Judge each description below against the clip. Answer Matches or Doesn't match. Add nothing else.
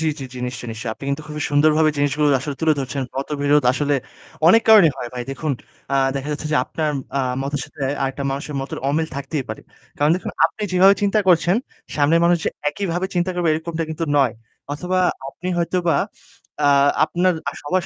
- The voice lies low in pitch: Doesn't match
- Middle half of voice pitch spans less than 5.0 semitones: Matches